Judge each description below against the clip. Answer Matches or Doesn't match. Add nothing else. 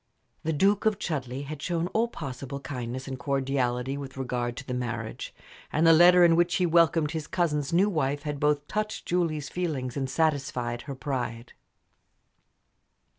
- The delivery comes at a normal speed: Matches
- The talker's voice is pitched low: Doesn't match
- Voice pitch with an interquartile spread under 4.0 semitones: Doesn't match